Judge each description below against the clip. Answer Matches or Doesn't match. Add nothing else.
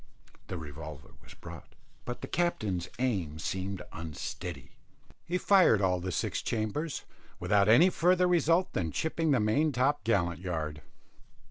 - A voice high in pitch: Doesn't match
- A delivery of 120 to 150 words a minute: Matches